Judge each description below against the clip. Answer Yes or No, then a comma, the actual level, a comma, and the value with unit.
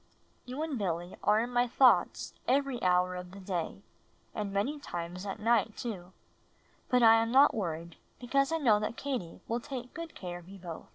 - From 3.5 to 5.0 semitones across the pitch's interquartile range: No, wide, 5.6 semitones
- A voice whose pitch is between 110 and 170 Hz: No, high, 215 Hz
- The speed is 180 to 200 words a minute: Yes, average, 190 wpm